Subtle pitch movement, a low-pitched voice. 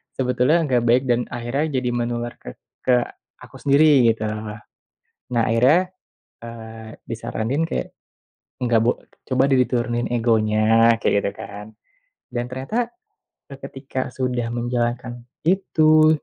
Yes: narrow, 2.3 semitones; low, 120 Hz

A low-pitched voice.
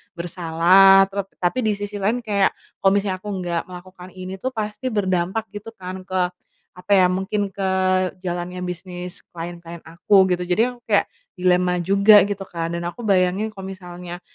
No: medium, 185 Hz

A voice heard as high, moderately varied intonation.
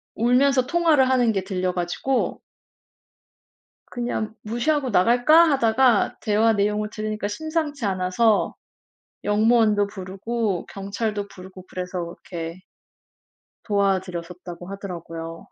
Yes: high, 210 Hz; average, 4.5 semitones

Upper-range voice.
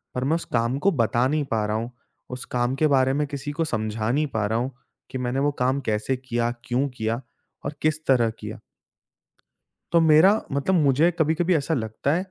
No: low, 130 Hz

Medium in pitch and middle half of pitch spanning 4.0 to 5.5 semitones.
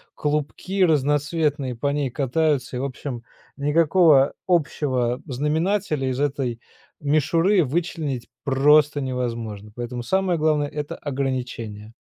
No: medium, 145 Hz; average, 3.4 semitones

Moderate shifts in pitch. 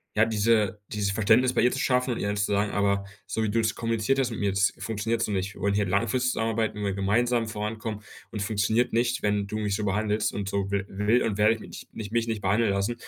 No: narrow, 2.1 semitones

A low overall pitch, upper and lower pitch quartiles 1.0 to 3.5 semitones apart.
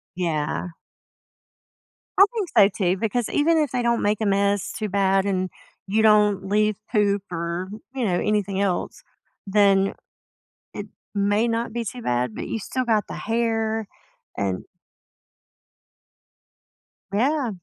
No: high, 205 Hz; average, 2.9 semitones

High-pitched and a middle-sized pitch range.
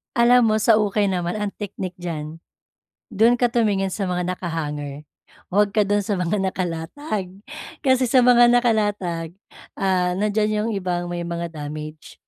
Yes: high, 195 Hz; average, 3.8 semitones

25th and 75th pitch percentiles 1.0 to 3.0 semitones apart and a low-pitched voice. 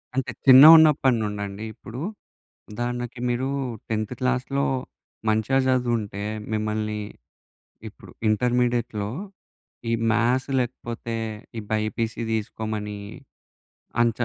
Yes: average, 2.7 semitones; low, 115 Hz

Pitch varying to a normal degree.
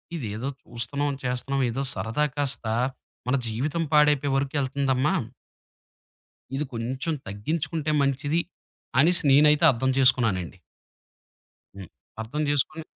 Yes: average, 3.2 semitones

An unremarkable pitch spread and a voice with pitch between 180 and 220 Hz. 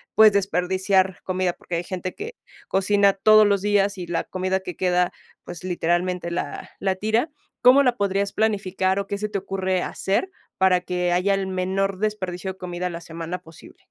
No: narrow, 1.9 semitones; high, 190 Hz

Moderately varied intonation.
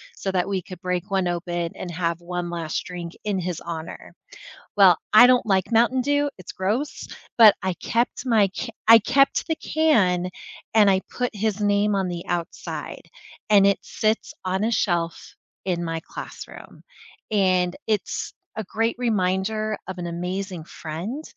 Yes: average, 3.7 semitones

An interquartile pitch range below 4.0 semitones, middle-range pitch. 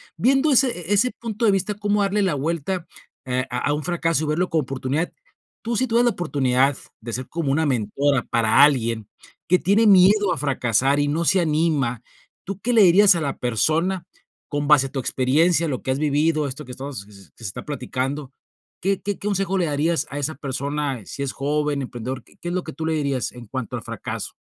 No: wide, 5.5 semitones; medium, 150 Hz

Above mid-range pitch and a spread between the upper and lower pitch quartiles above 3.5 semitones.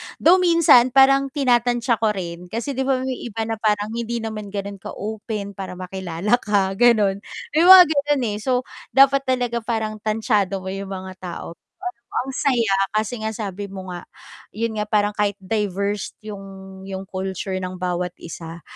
Yes: high, 210 Hz; average, 3.9 semitones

